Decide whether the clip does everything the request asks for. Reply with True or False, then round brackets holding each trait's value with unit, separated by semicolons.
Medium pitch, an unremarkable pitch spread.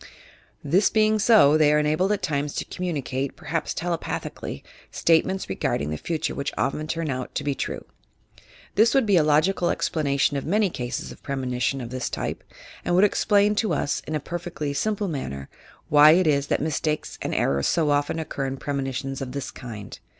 True (150 Hz; 4.4 semitones)